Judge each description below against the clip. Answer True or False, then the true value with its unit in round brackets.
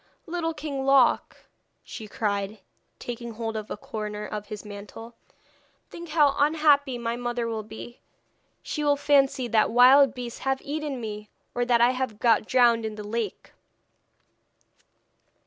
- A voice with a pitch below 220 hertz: False (240 Hz)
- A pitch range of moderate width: True (4.2 semitones)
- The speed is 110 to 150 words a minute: True (145 wpm)